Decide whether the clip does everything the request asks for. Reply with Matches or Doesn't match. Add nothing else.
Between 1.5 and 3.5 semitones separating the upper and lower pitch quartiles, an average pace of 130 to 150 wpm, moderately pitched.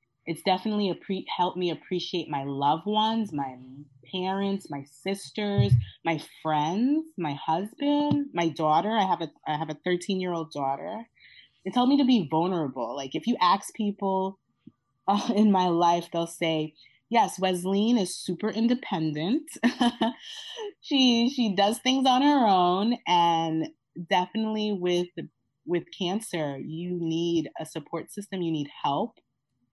Doesn't match